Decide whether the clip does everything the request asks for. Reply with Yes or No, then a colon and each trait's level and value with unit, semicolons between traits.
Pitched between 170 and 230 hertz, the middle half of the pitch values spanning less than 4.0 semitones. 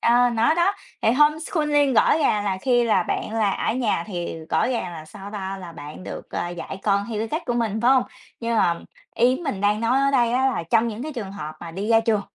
No: high, 225 Hz; average, 4.6 semitones